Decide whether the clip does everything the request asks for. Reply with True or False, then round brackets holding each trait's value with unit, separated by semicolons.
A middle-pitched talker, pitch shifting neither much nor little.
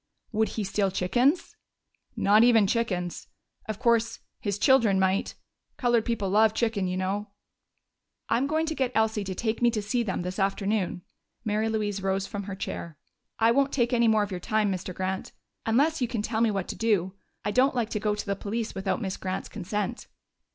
False (210 Hz; 3.1 semitones)